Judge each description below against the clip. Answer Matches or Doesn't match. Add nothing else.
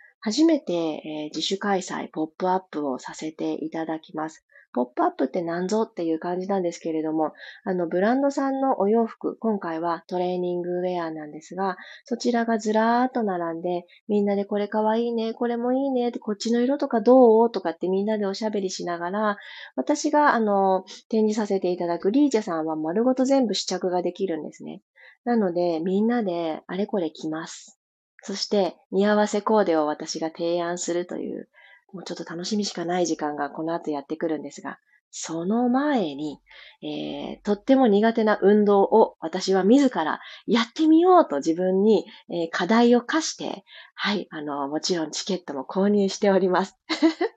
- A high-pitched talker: Matches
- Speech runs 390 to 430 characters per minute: Doesn't match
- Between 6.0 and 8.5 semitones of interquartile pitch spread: Doesn't match